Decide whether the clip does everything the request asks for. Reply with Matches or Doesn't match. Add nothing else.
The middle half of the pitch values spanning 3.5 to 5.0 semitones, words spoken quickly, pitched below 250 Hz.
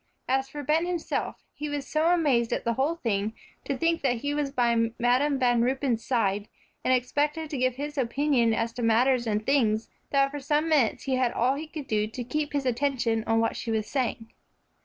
Doesn't match